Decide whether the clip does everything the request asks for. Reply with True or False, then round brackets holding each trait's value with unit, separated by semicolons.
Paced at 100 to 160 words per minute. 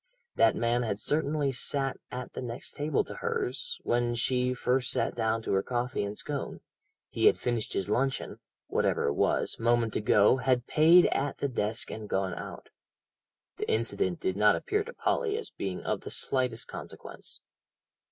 False (170 wpm)